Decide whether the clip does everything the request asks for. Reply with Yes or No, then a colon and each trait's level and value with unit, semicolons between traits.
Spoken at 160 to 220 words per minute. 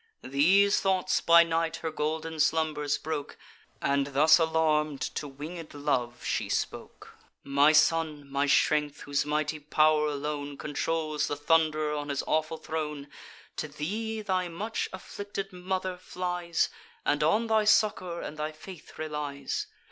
No: average, 140 wpm